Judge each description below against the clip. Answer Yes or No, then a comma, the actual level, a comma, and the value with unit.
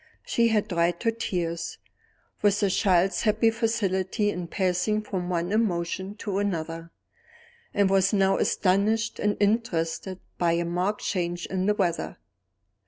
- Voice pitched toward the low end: No, high, 190 Hz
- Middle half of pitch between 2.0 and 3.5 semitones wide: Yes, average, 3.2 semitones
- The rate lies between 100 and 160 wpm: Yes, average, 140 wpm